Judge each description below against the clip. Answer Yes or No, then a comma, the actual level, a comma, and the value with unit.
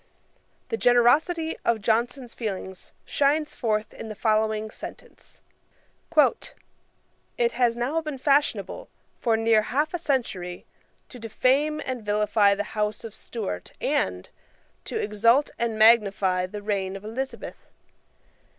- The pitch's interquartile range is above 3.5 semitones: Yes, average, 4.2 semitones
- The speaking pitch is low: No, high, 225 Hz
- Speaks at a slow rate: Yes, slow, 125 wpm